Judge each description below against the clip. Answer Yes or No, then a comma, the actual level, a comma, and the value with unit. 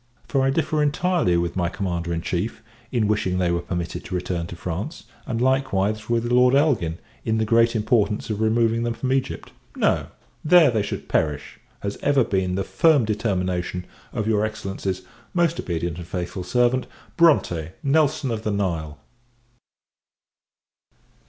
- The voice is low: Yes, low, 110 Hz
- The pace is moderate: Yes, average, 160 wpm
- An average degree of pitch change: No, wide, 5.8 semitones